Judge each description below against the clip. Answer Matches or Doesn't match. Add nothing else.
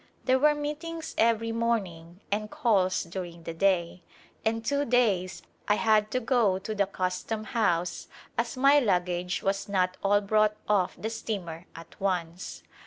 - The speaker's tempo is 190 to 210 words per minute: Doesn't match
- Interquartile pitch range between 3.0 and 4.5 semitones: Matches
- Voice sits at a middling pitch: Doesn't match